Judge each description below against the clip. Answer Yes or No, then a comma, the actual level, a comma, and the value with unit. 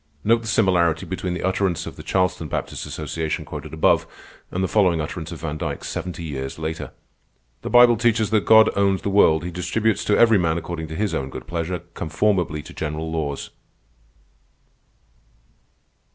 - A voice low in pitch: Yes, very low, 85 Hz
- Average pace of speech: Yes, average, 170 wpm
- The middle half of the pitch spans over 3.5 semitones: Yes, average, 4.0 semitones